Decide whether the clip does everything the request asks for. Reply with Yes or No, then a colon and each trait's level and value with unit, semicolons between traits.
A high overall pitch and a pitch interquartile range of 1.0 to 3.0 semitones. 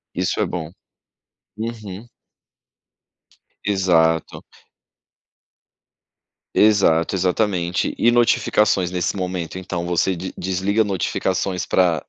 No: very low, 95 Hz; average, 2.7 semitones